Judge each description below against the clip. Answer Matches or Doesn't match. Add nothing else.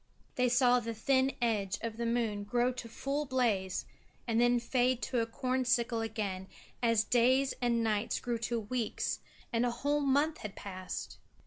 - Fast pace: Doesn't match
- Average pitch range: Doesn't match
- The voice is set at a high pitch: Matches